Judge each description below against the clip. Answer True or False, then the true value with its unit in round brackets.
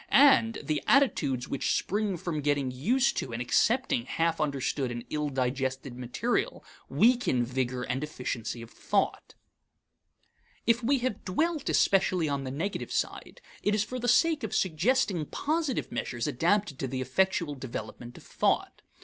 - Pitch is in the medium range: True (155 Hz)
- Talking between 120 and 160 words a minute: True (150 wpm)